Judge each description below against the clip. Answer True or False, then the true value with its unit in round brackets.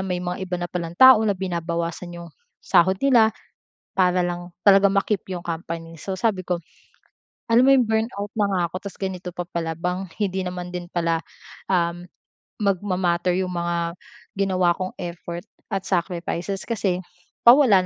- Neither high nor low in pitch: True (180 Hz)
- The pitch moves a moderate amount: False (2.1 semitones)